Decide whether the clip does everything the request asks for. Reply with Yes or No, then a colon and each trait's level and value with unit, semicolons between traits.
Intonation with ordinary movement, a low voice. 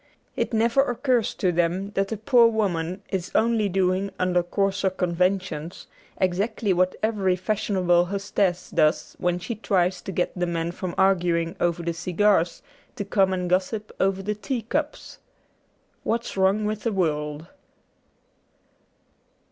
No: average, 3.0 semitones; high, 190 Hz